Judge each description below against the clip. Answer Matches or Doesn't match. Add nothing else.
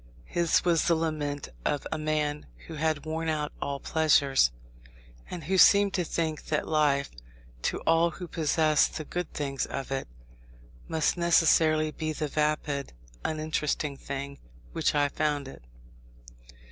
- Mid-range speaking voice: Matches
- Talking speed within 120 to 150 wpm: Matches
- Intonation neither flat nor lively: Doesn't match